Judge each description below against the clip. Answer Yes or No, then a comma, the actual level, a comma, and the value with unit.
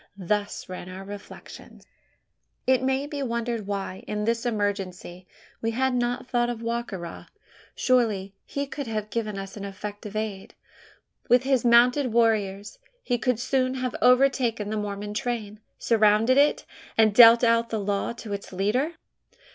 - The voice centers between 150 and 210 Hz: No, high, 225 Hz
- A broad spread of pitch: No, average, 3.3 semitones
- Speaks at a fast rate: No, average, 155 wpm